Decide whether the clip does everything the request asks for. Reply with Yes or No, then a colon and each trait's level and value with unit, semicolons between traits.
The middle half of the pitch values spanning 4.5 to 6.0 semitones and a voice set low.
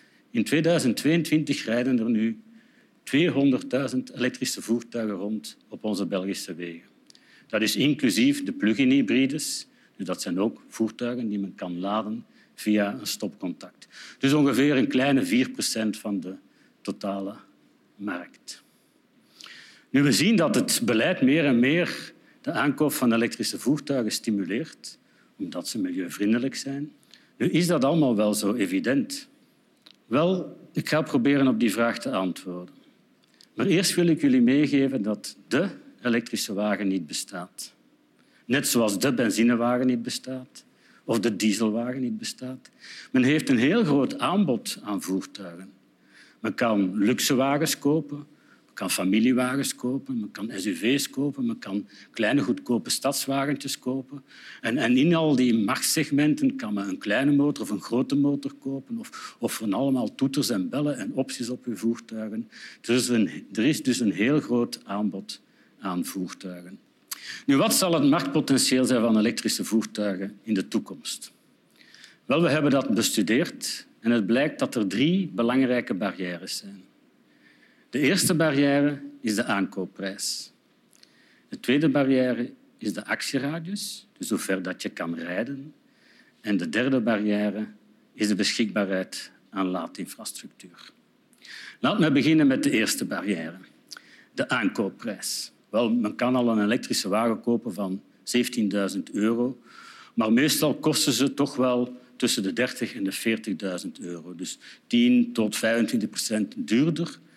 Yes: wide, 5.6 semitones; low, 125 Hz